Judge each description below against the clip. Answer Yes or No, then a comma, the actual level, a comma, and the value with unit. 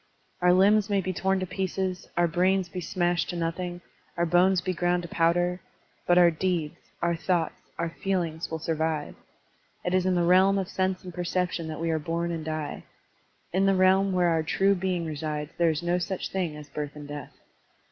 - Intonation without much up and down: Yes, narrow, 2.2 semitones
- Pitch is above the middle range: No, medium, 175 Hz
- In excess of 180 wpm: Yes, fast, 205 wpm